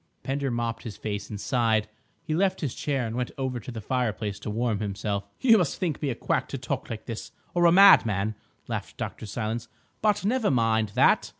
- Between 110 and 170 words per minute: No, fast, 205 wpm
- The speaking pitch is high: No, low, 120 Hz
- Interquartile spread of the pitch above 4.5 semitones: Yes, average, 5.2 semitones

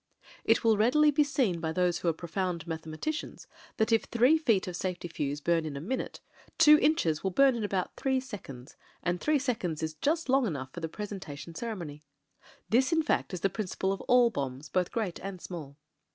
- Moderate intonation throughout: No, wide, 7.4 semitones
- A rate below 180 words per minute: No, fast, 205 wpm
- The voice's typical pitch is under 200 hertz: Yes, high, 190 Hz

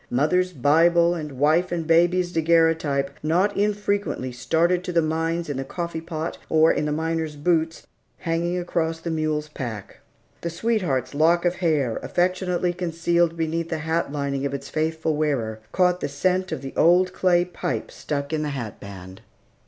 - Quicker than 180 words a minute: No, average, 170 wpm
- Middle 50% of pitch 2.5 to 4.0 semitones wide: Yes, average, 2.9 semitones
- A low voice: No, medium, 165 Hz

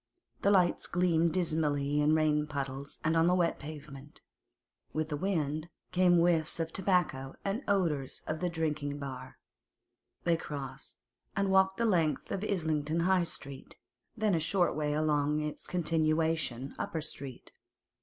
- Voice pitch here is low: No, medium, 155 Hz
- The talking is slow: No, average, 145 wpm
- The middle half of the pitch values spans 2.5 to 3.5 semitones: Yes, average, 3.0 semitones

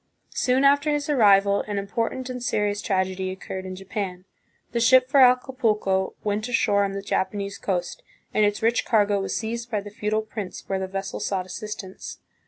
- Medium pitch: No, high, 205 Hz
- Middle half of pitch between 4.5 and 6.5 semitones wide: No, average, 3.3 semitones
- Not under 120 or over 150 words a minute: No, average, 185 wpm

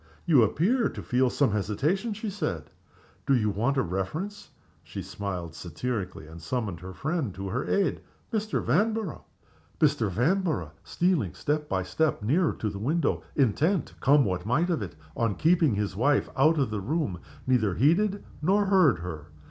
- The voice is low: Yes, low, 130 Hz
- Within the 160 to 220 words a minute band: Yes, average, 165 wpm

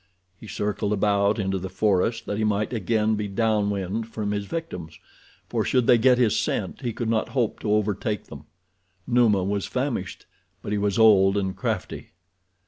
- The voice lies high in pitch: No, low, 105 Hz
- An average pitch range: No, narrow, 2.3 semitones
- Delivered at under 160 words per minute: No, average, 180 wpm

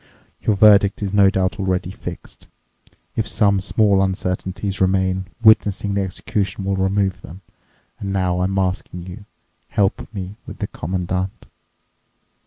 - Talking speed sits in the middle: No, slow, 130 wpm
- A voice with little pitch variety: Yes, narrow, 1.3 semitones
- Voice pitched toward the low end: Yes, very low, 95 Hz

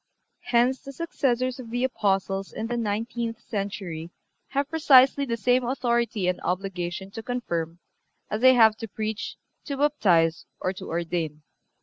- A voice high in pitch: Yes, high, 225 Hz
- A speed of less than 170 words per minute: Yes, average, 145 wpm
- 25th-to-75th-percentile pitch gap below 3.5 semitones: No, average, 4.8 semitones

